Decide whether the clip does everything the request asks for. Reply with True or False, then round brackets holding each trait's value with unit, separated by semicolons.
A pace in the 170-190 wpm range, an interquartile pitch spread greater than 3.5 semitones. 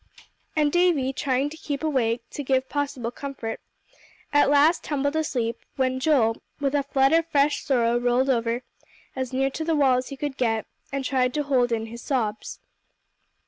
False (180 wpm; 2.8 semitones)